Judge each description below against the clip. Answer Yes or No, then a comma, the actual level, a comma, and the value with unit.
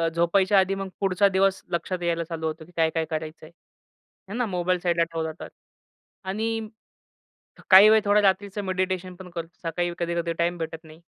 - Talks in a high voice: No, medium, 180 Hz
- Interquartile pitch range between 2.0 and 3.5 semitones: Yes, narrow, 2.6 semitones